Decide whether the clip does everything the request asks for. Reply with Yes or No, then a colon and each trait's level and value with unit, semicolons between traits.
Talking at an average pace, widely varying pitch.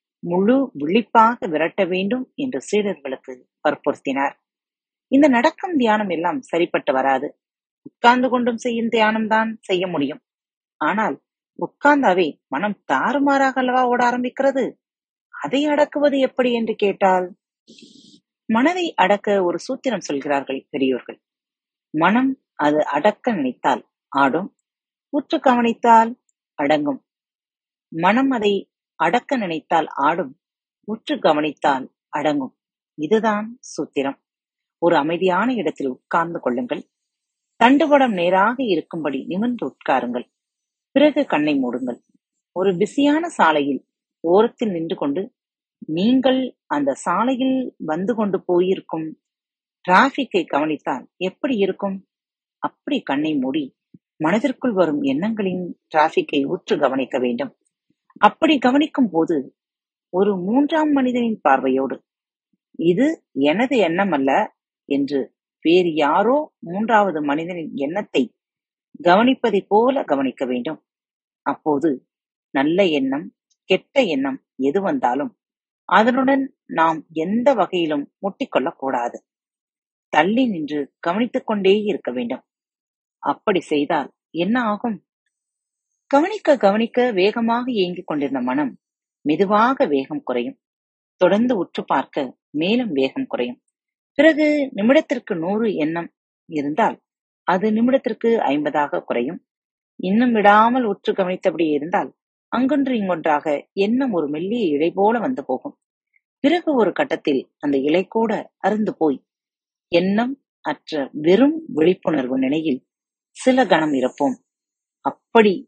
Yes: average, 100 wpm; wide, 7.5 semitones